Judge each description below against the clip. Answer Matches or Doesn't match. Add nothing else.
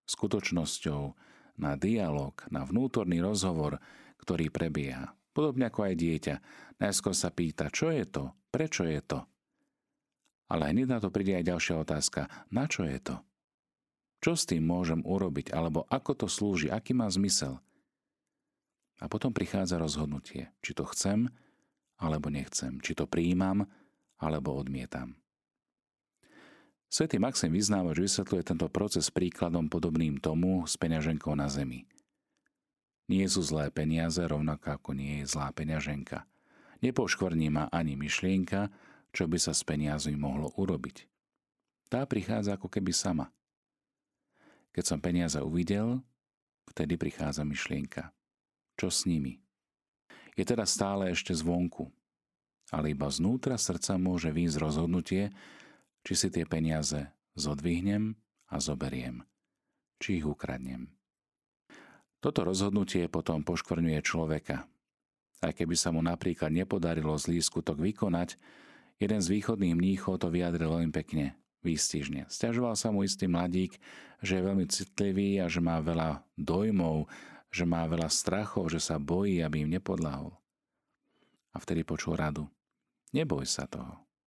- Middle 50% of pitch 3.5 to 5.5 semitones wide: Matches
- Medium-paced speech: Matches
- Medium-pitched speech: Doesn't match